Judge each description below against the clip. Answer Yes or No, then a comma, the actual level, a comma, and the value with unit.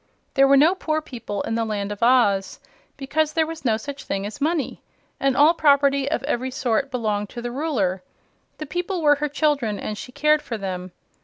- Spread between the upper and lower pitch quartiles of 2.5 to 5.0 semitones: No, wide, 5.4 semitones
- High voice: Yes, very high, 275 Hz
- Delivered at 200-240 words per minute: Yes, fast, 205 wpm